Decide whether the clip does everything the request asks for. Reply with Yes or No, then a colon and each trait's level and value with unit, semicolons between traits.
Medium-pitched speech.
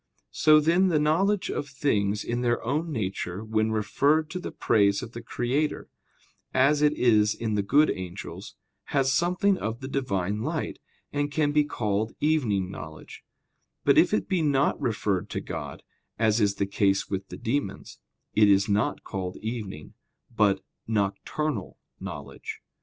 No: low, 115 Hz